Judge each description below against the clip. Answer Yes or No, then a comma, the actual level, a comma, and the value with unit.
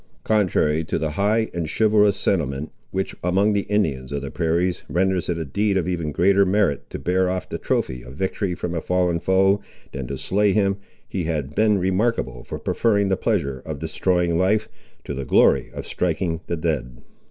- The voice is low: Yes, very low, 90 Hz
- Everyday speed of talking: Yes, average, 190 wpm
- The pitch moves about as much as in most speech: Yes, average, 4.2 semitones